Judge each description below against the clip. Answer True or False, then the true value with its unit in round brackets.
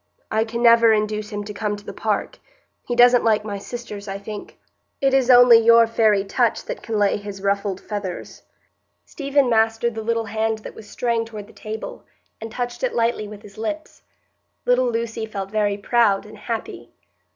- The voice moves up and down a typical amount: False (2.1 semitones)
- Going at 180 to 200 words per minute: True (185 wpm)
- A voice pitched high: True (220 Hz)